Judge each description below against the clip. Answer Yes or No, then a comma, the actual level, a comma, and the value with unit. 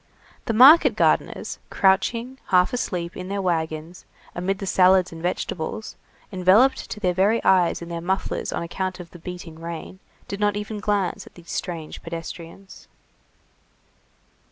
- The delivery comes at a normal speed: Yes, average, 150 wpm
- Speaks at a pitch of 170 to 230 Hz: Yes, medium, 185 Hz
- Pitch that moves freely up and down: No, average, 2.9 semitones